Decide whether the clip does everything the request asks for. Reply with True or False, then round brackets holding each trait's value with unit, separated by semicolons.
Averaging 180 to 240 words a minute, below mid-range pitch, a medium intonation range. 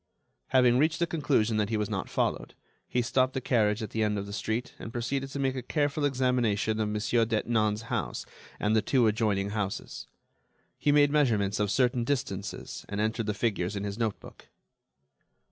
True (185 wpm; 115 Hz; 3.5 semitones)